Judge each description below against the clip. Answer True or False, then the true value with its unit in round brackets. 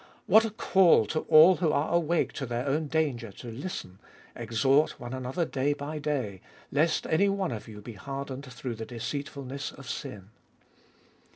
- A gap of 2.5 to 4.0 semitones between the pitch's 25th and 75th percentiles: False (4.8 semitones)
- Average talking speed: True (175 wpm)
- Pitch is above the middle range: False (140 Hz)